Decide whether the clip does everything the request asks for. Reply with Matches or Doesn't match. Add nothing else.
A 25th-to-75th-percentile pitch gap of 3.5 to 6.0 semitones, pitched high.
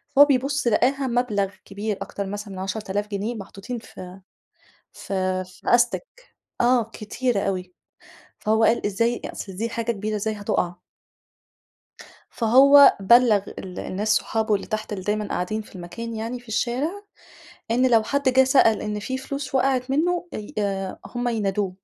Matches